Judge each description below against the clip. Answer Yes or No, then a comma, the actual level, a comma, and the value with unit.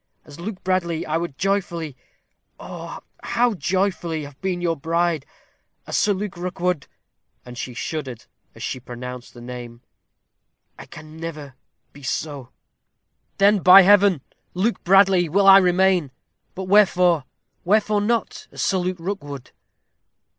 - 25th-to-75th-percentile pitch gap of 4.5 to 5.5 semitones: Yes, average, 4.9 semitones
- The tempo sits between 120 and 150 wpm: Yes, slow, 135 wpm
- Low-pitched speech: No, medium, 175 Hz